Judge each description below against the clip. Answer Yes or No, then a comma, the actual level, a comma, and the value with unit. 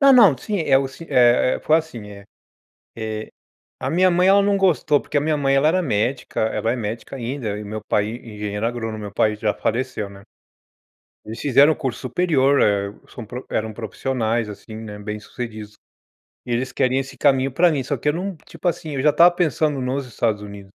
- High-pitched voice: No, low, 125 Hz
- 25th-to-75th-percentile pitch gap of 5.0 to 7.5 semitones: Yes, wide, 5.5 semitones